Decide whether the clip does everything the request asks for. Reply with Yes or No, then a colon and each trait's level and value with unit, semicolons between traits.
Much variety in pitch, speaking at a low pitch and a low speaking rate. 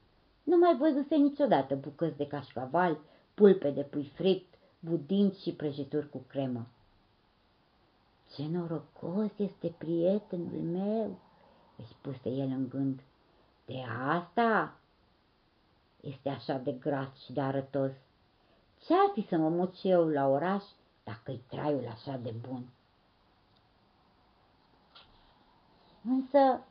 No: wide, 5.9 semitones; medium, 145 Hz; slow, 110 wpm